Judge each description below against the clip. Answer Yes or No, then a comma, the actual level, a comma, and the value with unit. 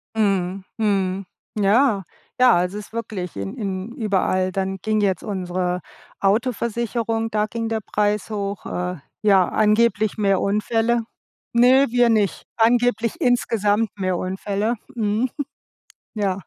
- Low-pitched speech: No, high, 210 Hz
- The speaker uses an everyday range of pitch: Yes, average, 3.0 semitones